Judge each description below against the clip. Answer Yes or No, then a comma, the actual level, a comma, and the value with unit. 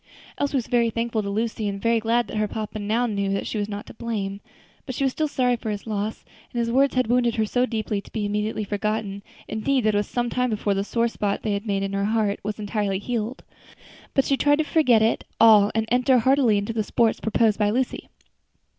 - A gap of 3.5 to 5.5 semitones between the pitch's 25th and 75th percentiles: No, average, 2.7 semitones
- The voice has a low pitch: No, high, 220 Hz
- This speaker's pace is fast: Yes, fast, 235 wpm